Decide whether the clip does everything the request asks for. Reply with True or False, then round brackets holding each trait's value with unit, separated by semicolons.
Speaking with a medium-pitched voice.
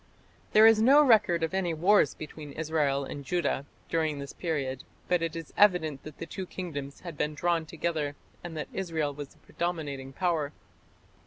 True (160 Hz)